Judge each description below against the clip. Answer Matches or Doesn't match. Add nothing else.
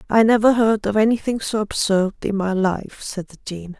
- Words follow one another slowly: Doesn't match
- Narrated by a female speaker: Matches